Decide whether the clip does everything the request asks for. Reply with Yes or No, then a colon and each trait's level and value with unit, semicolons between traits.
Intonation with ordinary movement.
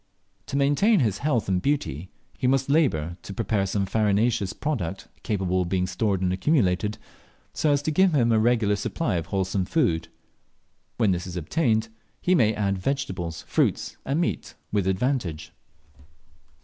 No: wide, 6.8 semitones